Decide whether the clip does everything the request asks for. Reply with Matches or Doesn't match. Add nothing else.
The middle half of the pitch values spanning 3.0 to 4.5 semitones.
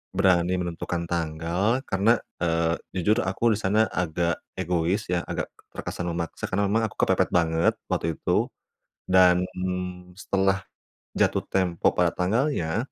Doesn't match